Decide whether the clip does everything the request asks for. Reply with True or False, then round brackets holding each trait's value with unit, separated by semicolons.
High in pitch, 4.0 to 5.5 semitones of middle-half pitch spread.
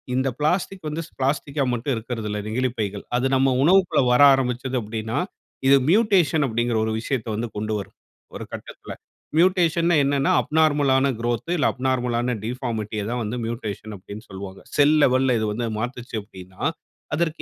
False (125 Hz; 4.6 semitones)